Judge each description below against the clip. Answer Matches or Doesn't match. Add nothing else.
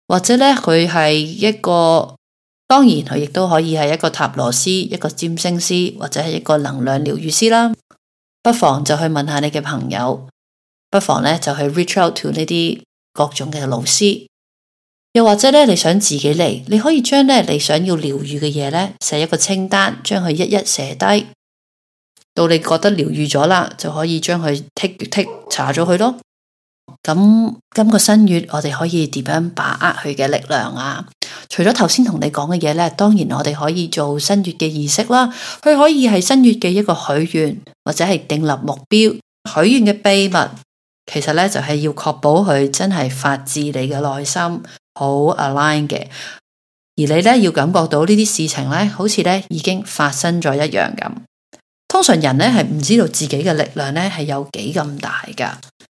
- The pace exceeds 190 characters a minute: Matches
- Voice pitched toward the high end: Doesn't match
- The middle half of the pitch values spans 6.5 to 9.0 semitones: Doesn't match